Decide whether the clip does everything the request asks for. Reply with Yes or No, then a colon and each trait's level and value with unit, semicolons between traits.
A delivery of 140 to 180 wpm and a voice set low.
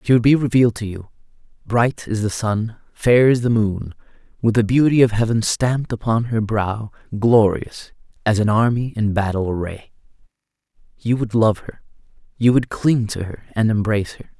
Yes: average, 175 wpm; low, 110 Hz